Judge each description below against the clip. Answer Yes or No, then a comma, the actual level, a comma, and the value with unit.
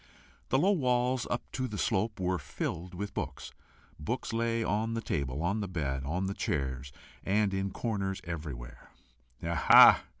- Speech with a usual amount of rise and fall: No, wide, 6.4 semitones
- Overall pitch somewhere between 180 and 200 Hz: No, very low, 95 Hz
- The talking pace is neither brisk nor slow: Yes, average, 155 wpm